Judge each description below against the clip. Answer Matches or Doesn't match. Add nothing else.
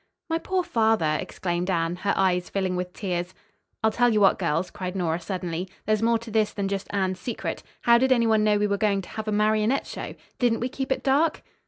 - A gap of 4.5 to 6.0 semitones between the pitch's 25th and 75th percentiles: Doesn't match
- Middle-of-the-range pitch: Doesn't match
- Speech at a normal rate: Doesn't match